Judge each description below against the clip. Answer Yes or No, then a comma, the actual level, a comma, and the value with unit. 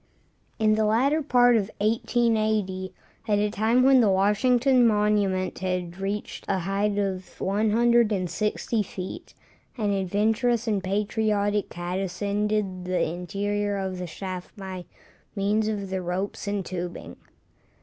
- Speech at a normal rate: No, slow, 130 wpm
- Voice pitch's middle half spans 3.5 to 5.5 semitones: No, narrow, 2.5 semitones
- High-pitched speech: Yes, high, 205 Hz